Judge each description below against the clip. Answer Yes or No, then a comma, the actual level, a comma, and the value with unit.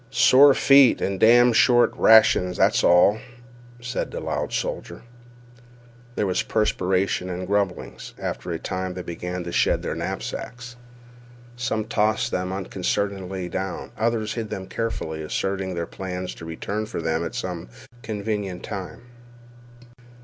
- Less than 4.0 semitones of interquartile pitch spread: Yes, average, 3.6 semitones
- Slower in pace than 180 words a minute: Yes, slow, 135 wpm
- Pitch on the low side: Yes, very low, 95 Hz